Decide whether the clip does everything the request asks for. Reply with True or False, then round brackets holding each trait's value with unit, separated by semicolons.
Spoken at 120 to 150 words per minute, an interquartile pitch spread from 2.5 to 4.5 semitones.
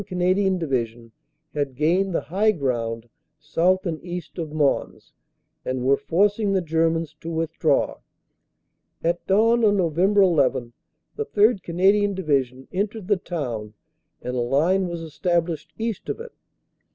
False (145 wpm; 5.4 semitones)